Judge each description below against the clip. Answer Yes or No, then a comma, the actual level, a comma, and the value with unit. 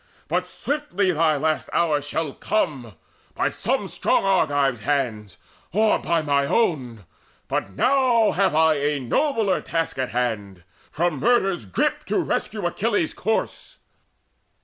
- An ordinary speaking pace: No, slow, 130 wpm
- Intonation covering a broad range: Yes, wide, 6.6 semitones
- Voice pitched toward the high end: No, medium, 155 Hz